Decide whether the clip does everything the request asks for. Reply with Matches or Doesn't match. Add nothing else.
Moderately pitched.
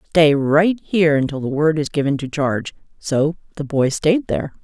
Matches